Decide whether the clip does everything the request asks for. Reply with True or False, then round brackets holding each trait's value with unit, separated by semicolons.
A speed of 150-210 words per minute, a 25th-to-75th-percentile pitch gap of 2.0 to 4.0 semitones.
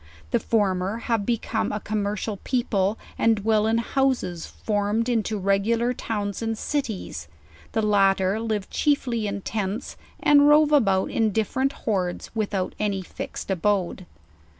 False (140 wpm; 2.7 semitones)